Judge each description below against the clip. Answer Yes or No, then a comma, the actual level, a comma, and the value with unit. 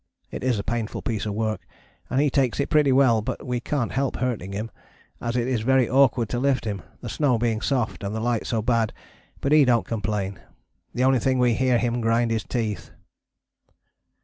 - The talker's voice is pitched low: Yes, low, 120 Hz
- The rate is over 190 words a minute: Yes, fast, 205 wpm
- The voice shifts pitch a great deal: No, average, 2.8 semitones